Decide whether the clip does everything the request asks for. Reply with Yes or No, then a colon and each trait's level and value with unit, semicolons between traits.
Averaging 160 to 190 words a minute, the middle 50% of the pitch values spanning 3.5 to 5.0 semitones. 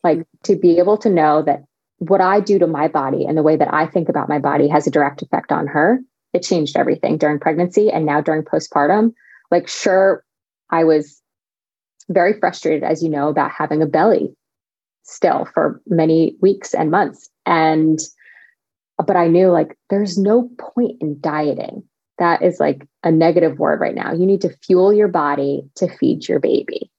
Yes: average, 185 wpm; average, 4.0 semitones